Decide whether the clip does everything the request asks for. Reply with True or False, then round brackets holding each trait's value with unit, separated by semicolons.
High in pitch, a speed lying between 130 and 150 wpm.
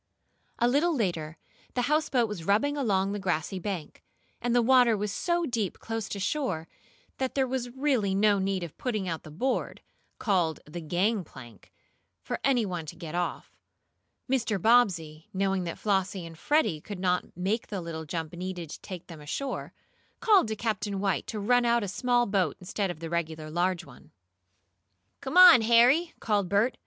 False (200 Hz; 175 wpm)